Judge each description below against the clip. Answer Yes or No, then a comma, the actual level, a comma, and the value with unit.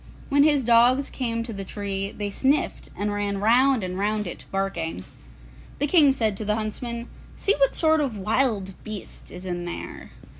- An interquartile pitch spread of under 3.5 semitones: No, average, 4.9 semitones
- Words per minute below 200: Yes, average, 185 wpm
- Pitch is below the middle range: No, high, 215 Hz